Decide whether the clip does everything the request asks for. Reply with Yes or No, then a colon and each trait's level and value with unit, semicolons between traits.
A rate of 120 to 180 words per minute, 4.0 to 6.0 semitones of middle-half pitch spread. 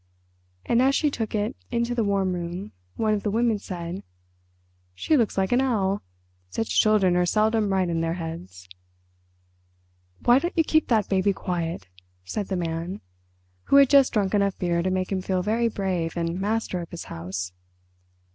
Yes: average, 175 wpm; average, 4.4 semitones